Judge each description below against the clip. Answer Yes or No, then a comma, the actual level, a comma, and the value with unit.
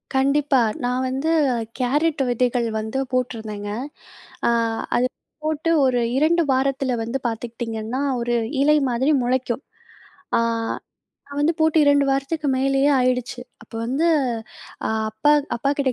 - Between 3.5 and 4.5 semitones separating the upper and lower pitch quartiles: No, average, 2.9 semitones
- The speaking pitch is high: Yes, very high, 260 Hz